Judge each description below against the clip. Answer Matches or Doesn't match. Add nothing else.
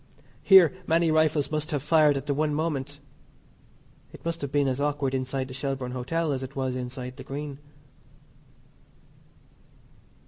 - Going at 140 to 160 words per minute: Matches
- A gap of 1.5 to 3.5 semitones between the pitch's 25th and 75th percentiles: Matches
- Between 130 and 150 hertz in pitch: Matches